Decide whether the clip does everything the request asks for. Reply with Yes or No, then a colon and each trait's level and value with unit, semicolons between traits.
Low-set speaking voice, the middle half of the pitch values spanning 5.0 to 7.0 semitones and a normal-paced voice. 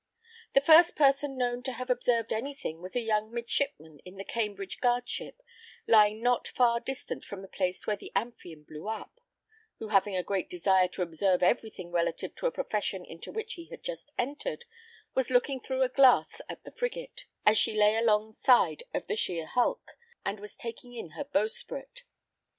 No: high, 230 Hz; wide, 5.5 semitones; average, 190 wpm